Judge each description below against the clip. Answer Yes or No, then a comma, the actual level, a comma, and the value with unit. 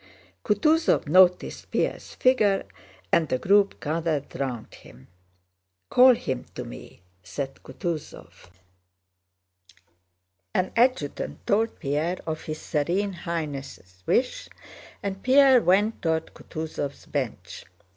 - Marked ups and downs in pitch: Yes, wide, 6.2 semitones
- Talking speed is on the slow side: Yes, slow, 105 wpm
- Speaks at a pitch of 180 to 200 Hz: No, medium, 170 Hz